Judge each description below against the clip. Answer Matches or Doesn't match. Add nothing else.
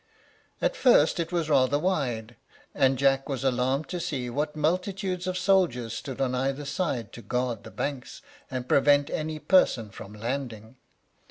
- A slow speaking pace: Doesn't match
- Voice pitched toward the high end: Doesn't match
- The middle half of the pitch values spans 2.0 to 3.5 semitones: Doesn't match